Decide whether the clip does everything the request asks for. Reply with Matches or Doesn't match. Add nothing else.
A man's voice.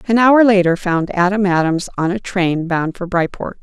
Doesn't match